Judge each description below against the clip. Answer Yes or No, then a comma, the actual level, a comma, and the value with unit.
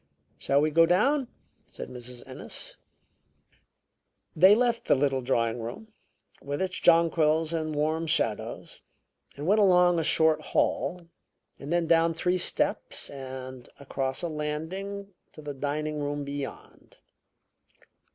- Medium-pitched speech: Yes, medium, 155 Hz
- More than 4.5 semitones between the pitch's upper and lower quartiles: No, average, 3.9 semitones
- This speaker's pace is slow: Yes, slow, 130 wpm